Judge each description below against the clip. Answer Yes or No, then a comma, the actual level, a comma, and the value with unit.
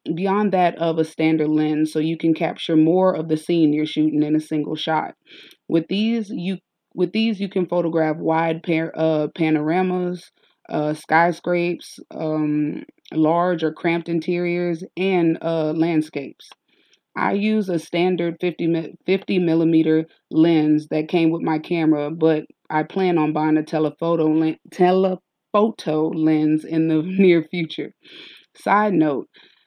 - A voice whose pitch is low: No, medium, 165 Hz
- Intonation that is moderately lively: No, narrow, 2.1 semitones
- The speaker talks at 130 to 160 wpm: Yes, average, 140 wpm